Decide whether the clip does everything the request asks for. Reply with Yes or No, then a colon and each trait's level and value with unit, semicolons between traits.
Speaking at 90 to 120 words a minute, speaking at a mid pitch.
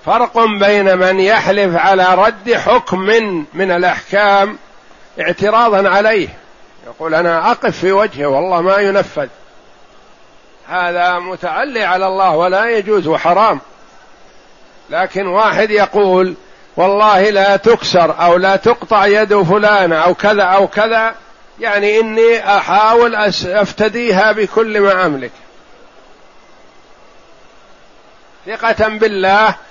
No: average, 100 wpm; high, 200 Hz